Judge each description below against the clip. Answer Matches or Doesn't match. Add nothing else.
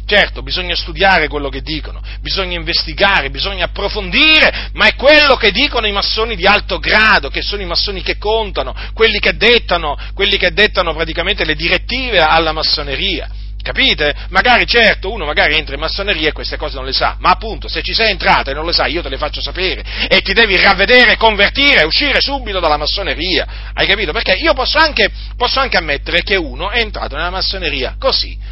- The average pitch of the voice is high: Matches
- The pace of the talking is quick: Matches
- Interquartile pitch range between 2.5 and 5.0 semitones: Doesn't match